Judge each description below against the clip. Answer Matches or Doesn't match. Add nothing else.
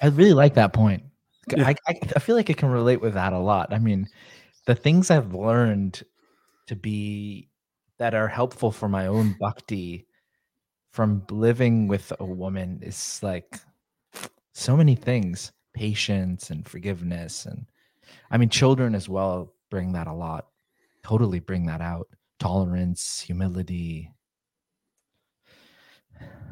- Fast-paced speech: Doesn't match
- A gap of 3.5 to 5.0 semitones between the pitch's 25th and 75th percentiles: Matches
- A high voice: Doesn't match